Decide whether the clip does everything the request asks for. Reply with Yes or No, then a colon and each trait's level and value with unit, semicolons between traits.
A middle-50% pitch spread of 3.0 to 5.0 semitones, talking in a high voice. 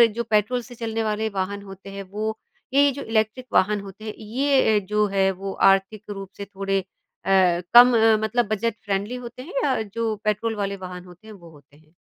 No: narrow, 2.6 semitones; high, 210 Hz